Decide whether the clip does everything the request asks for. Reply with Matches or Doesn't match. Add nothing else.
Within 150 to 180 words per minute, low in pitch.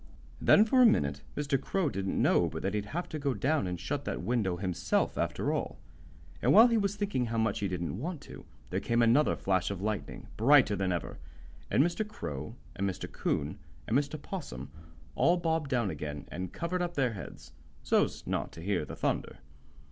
Doesn't match